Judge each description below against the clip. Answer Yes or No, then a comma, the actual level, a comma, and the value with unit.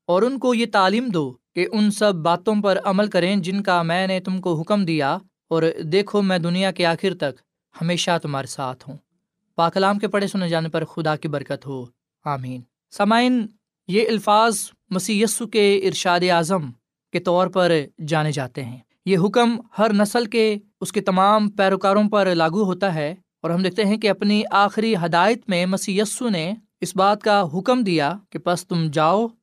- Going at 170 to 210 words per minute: Yes, average, 185 wpm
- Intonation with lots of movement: No, average, 4.0 semitones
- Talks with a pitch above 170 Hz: Yes, high, 190 Hz